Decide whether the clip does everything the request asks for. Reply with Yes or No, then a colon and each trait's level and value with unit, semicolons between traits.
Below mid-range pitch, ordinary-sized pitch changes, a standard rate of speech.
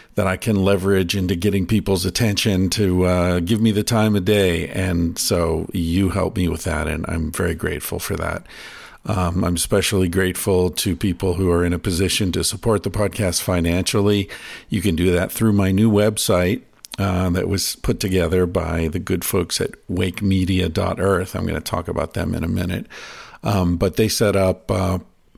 No: very low, 95 Hz; narrow, 2.3 semitones; average, 185 wpm